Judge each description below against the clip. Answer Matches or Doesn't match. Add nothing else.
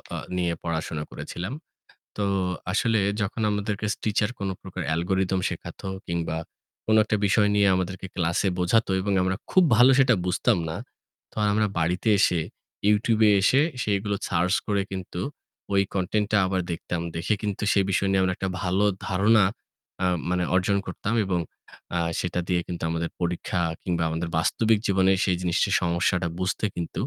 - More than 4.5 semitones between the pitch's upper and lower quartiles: Doesn't match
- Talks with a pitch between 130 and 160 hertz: Doesn't match